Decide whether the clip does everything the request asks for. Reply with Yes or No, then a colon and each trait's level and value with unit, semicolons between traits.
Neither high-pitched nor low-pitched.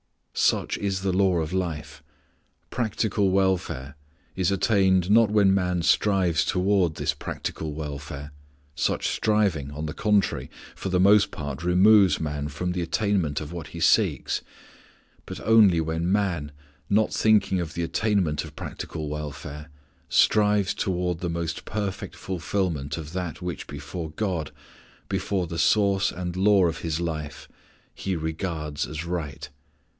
No: very low, 90 Hz